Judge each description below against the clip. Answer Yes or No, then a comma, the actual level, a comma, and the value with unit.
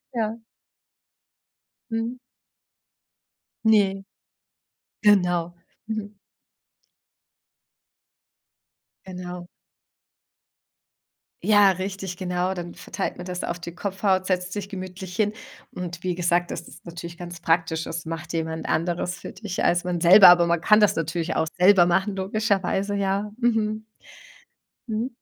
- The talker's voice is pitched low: No, medium, 185 Hz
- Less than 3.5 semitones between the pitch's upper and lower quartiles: Yes, average, 2.7 semitones